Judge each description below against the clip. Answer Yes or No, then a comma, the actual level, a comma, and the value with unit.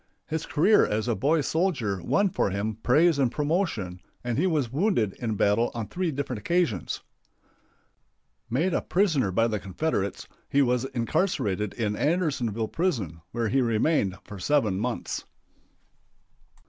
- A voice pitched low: Yes, low, 125 Hz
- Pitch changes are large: Yes, wide, 7.2 semitones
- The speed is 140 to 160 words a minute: Yes, average, 145 wpm